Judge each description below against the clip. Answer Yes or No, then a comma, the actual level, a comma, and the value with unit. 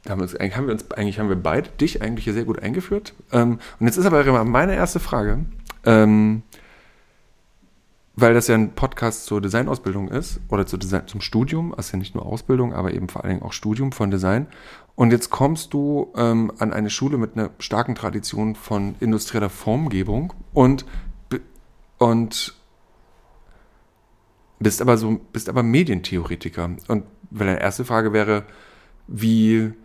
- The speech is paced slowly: No, average, 145 wpm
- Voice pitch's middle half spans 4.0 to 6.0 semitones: No, average, 2.9 semitones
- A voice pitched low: Yes, low, 110 Hz